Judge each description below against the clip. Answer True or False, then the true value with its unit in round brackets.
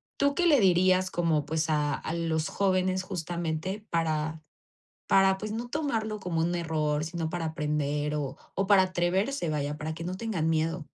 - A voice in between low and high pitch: True (170 Hz)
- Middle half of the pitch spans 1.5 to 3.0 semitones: False (3.4 semitones)